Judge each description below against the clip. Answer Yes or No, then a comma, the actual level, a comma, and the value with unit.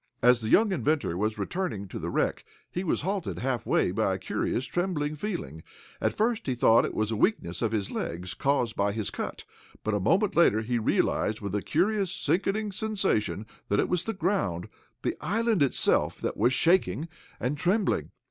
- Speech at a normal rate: Yes, average, 185 wpm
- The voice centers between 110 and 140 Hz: Yes, low, 135 Hz